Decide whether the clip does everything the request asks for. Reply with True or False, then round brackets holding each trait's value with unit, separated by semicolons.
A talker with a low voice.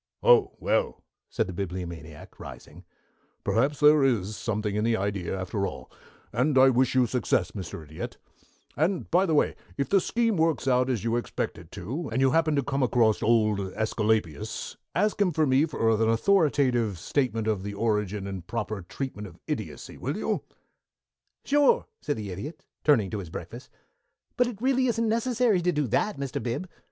True (120 Hz)